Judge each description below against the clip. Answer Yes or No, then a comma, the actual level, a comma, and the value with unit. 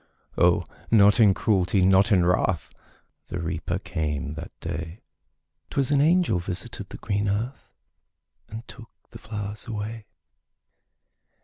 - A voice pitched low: Yes, low, 100 Hz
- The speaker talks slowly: Yes, slow, 125 wpm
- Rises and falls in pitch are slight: No, average, 4.1 semitones